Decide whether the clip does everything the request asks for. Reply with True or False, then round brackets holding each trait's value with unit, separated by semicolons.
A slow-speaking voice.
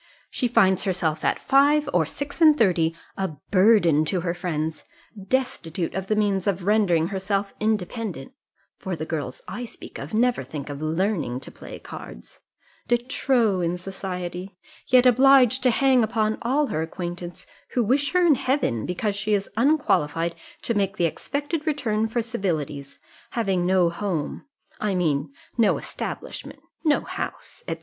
False (155 wpm)